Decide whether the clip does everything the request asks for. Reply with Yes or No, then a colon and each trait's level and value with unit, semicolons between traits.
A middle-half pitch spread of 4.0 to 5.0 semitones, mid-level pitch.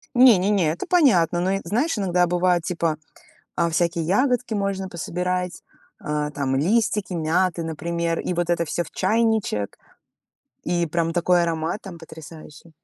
No: average, 2.8 semitones; medium, 175 Hz